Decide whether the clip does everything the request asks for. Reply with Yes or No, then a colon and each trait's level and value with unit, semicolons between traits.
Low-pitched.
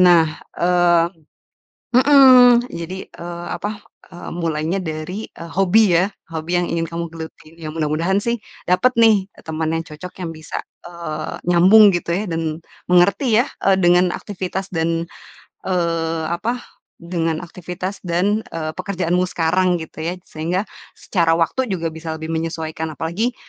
No: medium, 175 Hz